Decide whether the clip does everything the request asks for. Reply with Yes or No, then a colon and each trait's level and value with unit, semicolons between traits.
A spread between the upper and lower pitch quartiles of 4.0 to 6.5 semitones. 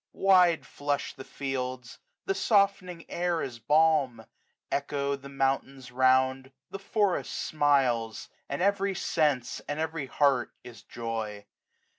Yes: average, 4.4 semitones